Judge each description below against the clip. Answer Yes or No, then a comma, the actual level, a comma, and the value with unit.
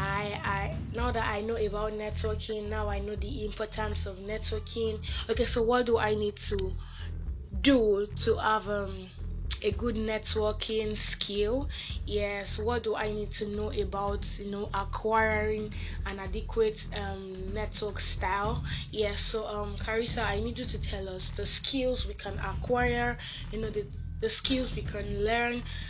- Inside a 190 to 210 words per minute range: No, average, 160 wpm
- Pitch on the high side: Yes, high, 210 Hz